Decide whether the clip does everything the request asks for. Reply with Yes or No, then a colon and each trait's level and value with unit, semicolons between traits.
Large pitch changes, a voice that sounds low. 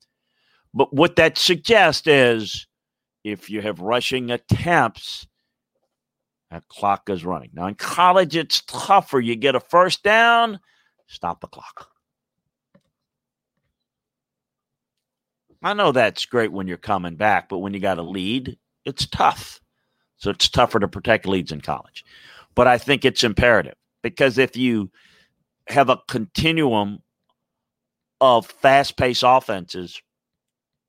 Yes: wide, 6.1 semitones; low, 120 Hz